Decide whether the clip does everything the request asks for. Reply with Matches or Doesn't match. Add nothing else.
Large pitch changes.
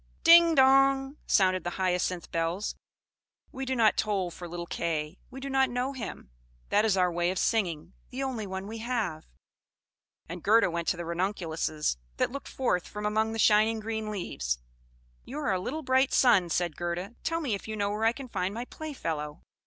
Matches